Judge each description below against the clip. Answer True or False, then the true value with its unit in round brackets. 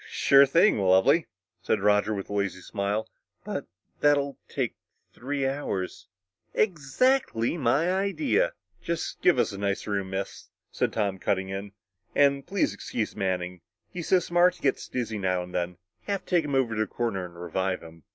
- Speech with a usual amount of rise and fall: False (7.4 semitones)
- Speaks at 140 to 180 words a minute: False (190 wpm)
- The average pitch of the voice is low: True (110 Hz)